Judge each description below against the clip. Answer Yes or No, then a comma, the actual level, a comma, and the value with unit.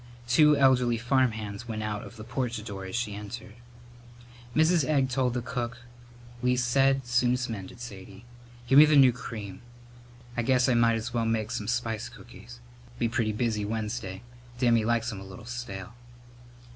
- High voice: No, low, 120 Hz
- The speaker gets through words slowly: No, average, 165 wpm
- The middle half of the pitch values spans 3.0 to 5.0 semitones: No, narrow, 2.6 semitones